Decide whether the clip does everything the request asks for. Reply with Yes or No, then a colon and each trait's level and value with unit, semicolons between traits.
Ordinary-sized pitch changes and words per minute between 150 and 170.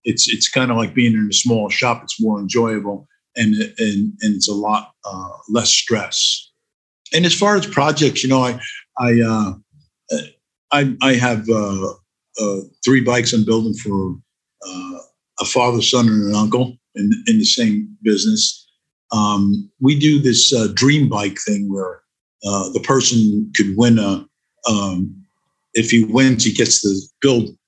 Yes: average, 4.9 semitones; average, 165 wpm